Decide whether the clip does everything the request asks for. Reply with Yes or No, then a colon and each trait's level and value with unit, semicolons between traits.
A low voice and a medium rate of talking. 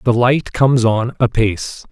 Yes: low, 120 Hz; average, 155 wpm